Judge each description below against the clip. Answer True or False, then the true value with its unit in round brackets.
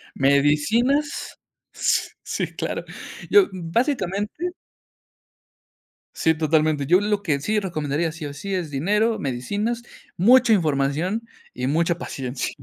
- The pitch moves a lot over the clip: True (6.5 semitones)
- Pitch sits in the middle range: True (170 Hz)